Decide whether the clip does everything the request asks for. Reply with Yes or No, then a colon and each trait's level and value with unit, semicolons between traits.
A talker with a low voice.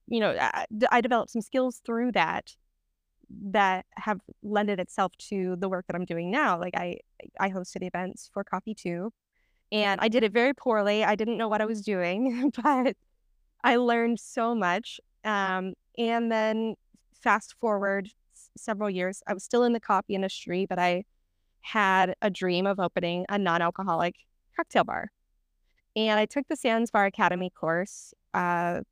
No: high, 205 Hz